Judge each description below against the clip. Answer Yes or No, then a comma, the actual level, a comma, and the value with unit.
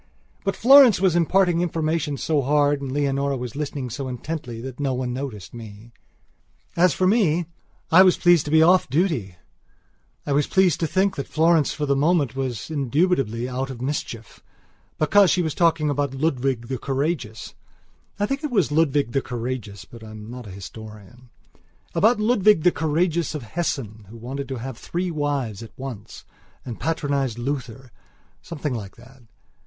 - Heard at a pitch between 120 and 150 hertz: Yes, medium, 140 Hz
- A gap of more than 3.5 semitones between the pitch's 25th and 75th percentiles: Yes, average, 5.2 semitones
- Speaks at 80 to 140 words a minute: No, average, 165 wpm